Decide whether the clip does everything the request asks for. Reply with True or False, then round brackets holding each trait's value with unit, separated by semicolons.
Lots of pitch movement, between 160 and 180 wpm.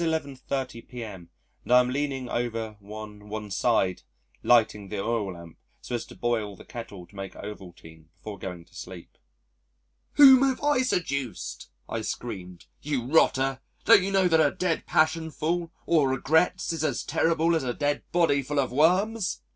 True (7.6 semitones; 170 wpm)